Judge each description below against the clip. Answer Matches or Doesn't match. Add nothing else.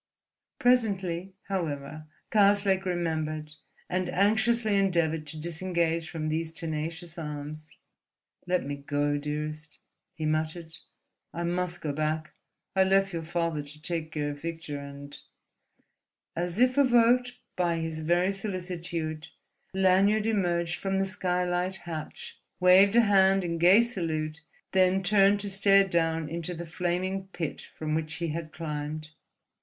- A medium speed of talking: Doesn't match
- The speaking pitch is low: Doesn't match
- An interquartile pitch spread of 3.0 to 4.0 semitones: Matches